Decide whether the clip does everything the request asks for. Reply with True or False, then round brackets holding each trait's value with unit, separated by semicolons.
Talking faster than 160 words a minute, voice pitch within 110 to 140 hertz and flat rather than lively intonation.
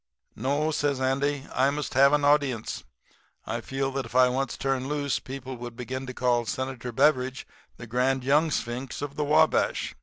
True (180 wpm; 135 Hz; 2.1 semitones)